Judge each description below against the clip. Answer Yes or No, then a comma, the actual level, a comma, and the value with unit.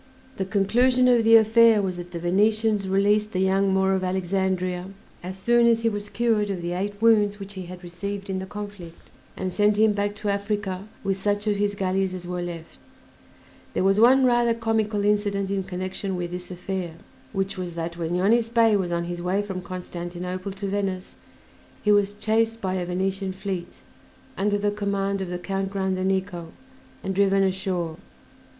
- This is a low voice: No, high, 195 Hz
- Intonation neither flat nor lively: No, narrow, 2.0 semitones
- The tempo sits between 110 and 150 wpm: No, average, 185 wpm